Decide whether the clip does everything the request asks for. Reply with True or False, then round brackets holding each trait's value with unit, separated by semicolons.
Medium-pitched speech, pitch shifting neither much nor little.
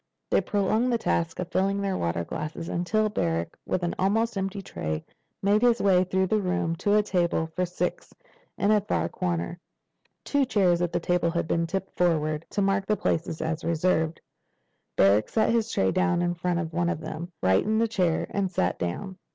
True (180 Hz; 3.3 semitones)